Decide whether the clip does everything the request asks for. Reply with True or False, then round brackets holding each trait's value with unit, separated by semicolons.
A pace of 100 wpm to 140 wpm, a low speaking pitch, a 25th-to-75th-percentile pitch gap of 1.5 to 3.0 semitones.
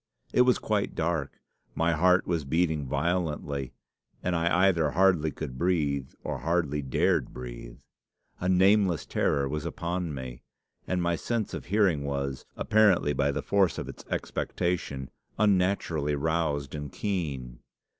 False (135 wpm; 80 Hz; 4.3 semitones)